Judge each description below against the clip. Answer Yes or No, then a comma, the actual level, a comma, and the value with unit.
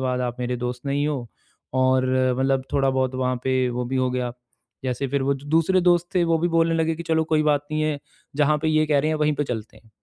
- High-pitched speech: No, medium, 140 Hz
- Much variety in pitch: No, average, 3.5 semitones